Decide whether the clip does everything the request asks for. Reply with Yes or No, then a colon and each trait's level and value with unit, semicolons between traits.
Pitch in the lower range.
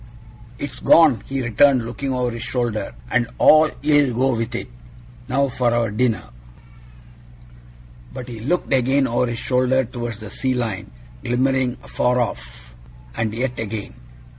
Yes: low, 125 Hz